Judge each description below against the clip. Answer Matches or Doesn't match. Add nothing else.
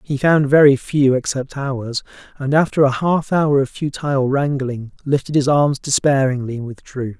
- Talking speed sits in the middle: Matches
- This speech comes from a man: Matches